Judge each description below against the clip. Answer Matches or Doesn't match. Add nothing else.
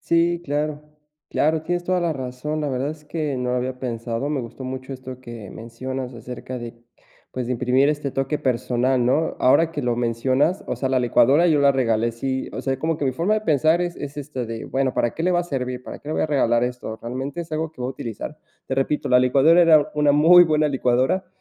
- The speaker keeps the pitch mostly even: Doesn't match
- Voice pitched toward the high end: Doesn't match